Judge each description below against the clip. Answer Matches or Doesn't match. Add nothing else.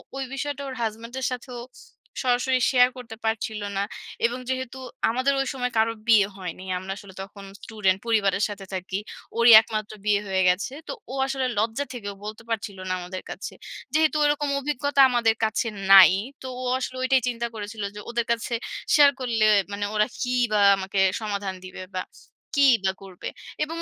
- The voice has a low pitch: Doesn't match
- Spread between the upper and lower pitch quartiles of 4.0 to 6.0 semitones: Matches